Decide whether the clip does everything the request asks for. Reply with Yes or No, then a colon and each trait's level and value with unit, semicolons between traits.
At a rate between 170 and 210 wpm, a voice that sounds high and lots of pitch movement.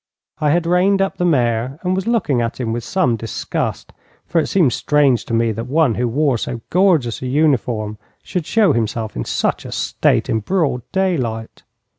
No: average, 190 wpm; low, 135 Hz; wide, 7.2 semitones